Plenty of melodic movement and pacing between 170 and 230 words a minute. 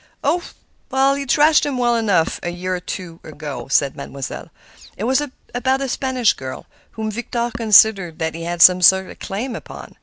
Yes: wide, 6.5 semitones; average, 180 wpm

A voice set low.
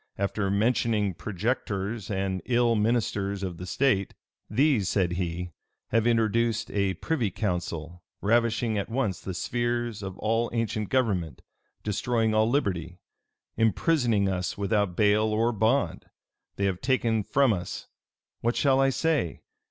Yes: low, 110 Hz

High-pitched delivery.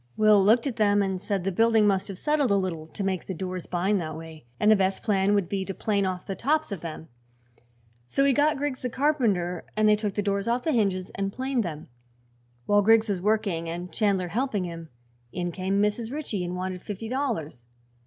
Yes: high, 200 Hz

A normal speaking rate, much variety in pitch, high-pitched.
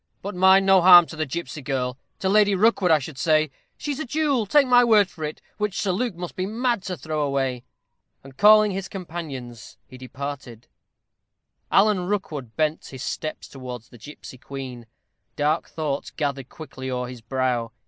No: average, 180 wpm; wide, 6.8 semitones; medium, 155 Hz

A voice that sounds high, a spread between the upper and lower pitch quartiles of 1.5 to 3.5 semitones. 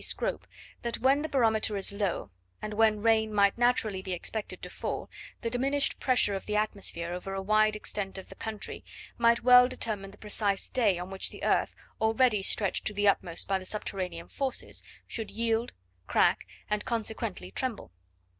Yes: high, 215 Hz; average, 2.9 semitones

